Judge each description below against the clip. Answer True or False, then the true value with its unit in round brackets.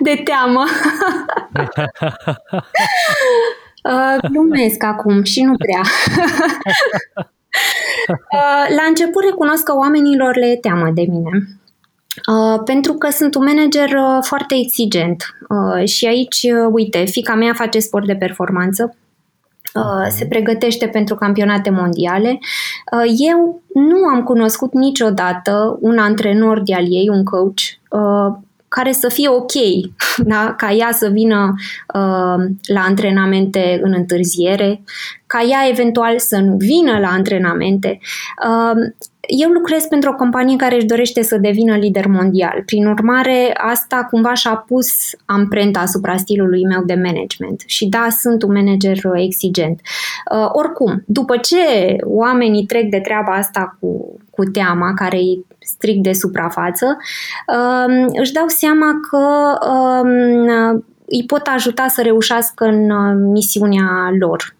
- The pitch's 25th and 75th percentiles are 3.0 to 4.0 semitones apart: False (4.8 semitones)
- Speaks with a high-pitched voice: True (225 Hz)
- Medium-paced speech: True (130 wpm)